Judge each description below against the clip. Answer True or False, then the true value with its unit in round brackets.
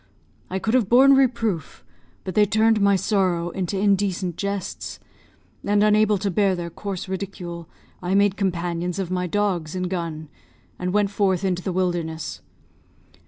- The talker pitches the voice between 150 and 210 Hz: True (190 Hz)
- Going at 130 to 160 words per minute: True (155 wpm)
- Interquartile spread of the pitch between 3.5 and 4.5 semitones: False (2.5 semitones)